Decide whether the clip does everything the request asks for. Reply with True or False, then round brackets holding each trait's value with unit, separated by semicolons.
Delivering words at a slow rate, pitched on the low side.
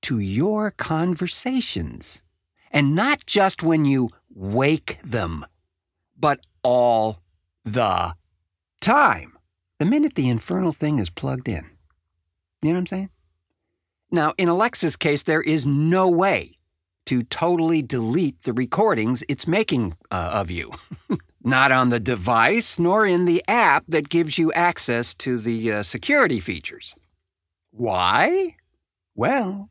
True (130 wpm; 125 Hz)